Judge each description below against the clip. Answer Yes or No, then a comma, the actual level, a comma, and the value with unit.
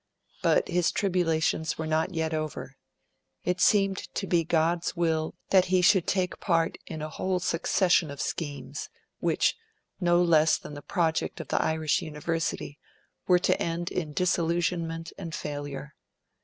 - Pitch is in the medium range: Yes, medium, 165 Hz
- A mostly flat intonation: Yes, narrow, 2.3 semitones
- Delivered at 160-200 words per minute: No, average, 150 wpm